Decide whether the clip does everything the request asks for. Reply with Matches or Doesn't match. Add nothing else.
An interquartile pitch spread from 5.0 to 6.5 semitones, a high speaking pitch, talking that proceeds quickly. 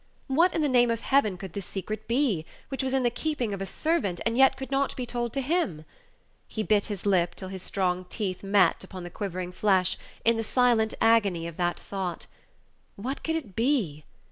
Matches